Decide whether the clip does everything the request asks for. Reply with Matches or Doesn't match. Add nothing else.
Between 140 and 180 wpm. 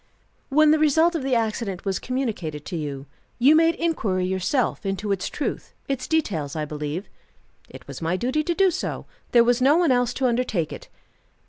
Doesn't match